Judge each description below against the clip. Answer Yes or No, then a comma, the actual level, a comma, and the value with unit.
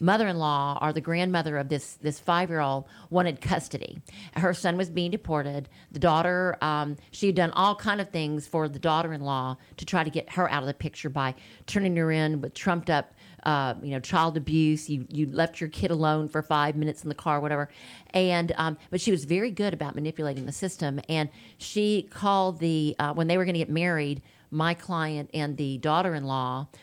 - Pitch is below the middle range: No, medium, 155 Hz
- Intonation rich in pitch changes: No, average, 3.2 semitones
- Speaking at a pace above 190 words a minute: Yes, average, 200 wpm